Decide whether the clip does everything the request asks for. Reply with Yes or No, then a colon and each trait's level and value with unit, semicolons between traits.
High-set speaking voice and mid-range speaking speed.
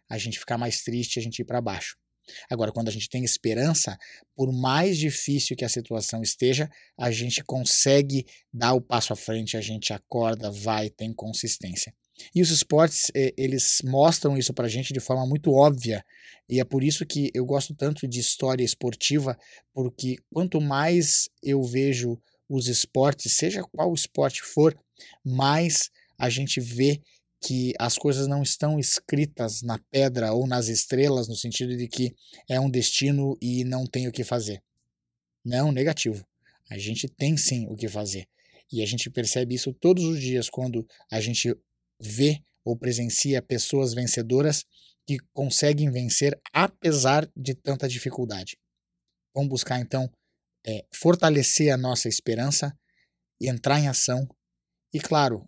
No: low, 125 Hz; average, 155 wpm